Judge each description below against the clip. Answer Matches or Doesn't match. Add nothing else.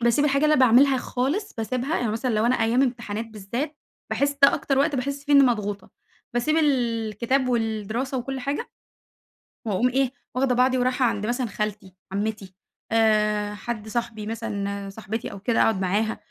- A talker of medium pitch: Doesn't match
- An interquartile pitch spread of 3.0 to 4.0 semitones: Matches